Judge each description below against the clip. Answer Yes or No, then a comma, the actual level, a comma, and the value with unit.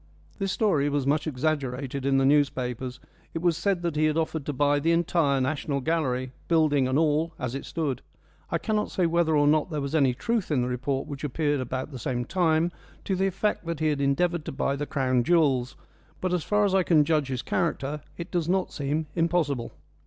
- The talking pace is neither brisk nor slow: No, fast, 215 wpm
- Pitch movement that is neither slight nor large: Yes, average, 3.6 semitones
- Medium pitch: Yes, medium, 150 Hz